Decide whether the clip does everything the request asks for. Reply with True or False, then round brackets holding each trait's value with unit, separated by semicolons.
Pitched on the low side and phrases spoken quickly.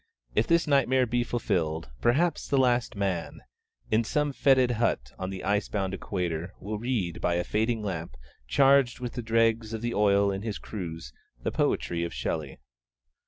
False (110 Hz; 170 wpm)